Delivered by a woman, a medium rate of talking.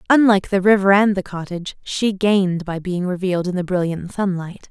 Yes: female; average, 190 wpm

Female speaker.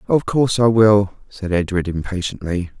No: male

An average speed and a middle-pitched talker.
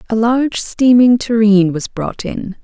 No: average, 160 wpm; high, 225 Hz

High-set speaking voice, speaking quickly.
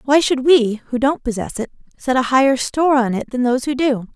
Yes: very high, 260 Hz; fast, 245 wpm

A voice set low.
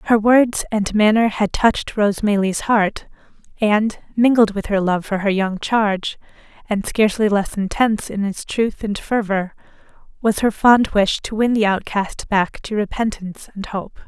No: high, 210 Hz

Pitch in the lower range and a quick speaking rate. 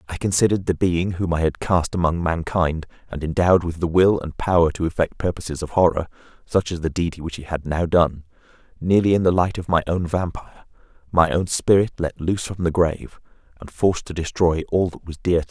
Yes: very low, 85 Hz; fast, 220 wpm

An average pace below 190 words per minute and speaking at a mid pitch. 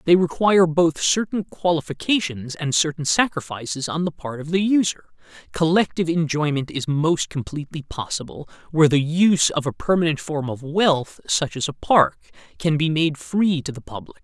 Yes: average, 170 wpm; medium, 155 Hz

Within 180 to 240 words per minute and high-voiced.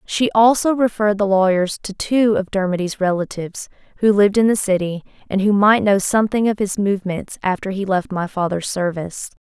Yes: average, 185 wpm; high, 200 Hz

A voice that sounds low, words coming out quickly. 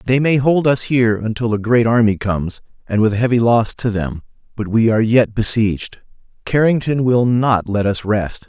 No: low, 115 Hz; average, 190 wpm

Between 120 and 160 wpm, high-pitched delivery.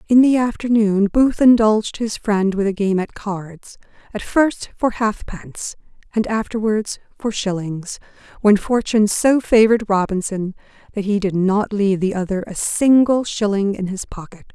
Yes: average, 155 wpm; high, 210 Hz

